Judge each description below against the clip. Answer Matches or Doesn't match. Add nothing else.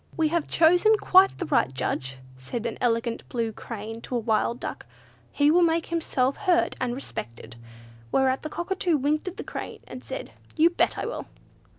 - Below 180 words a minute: Doesn't match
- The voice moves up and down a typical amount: Doesn't match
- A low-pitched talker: Doesn't match